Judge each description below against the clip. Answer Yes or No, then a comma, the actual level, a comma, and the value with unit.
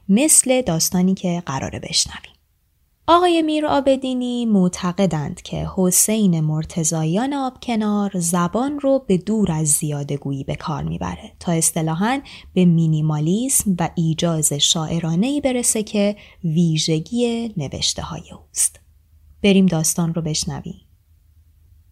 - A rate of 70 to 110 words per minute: Yes, slow, 105 wpm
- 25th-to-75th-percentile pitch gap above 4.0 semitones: Yes, wide, 5.5 semitones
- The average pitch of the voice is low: No, medium, 175 Hz